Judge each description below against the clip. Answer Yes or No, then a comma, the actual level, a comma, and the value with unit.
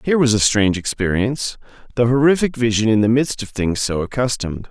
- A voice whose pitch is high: No, low, 115 Hz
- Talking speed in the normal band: Yes, average, 180 wpm